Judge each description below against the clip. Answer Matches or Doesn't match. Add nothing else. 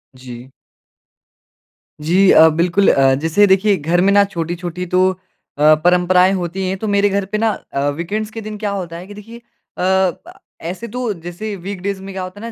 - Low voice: Doesn't match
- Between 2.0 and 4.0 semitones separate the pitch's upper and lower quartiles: Matches